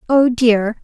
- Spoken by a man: No, female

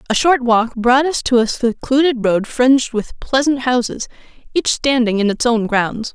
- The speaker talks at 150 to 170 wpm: No, average, 185 wpm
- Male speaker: No, female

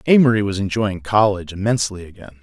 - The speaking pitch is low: Yes, low, 105 Hz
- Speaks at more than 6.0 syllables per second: Yes, 6.8 syllables/s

